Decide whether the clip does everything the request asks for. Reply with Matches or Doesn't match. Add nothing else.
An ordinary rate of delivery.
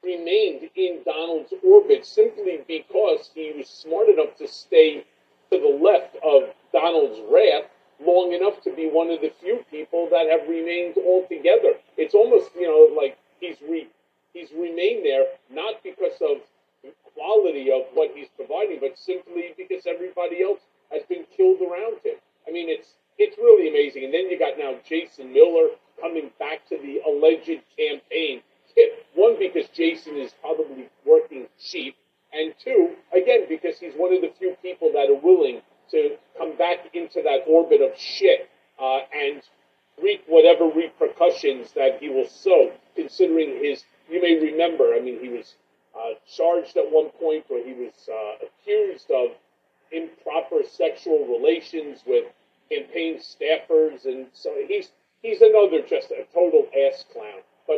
Matches